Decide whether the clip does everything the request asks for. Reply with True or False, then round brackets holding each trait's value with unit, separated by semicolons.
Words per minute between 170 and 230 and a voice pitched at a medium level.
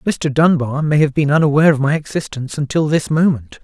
True (200 wpm; 145 Hz)